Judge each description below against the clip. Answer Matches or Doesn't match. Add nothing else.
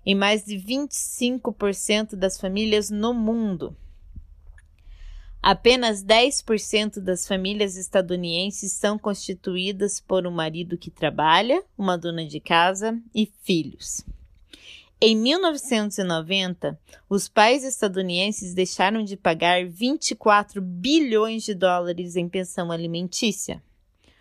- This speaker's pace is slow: Matches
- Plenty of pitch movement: Doesn't match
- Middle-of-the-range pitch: Doesn't match